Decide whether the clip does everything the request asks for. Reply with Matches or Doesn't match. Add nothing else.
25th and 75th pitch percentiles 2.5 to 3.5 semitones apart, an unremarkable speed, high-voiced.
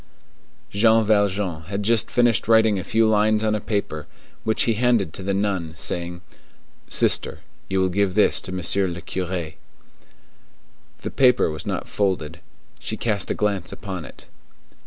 Doesn't match